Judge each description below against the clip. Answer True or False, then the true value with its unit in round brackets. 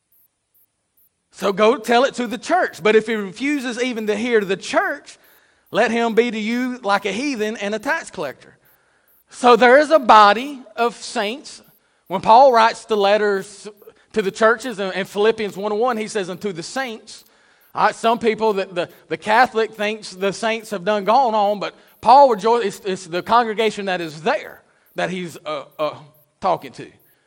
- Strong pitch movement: False (3.3 semitones)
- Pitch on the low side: False (215 Hz)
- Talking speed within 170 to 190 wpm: True (180 wpm)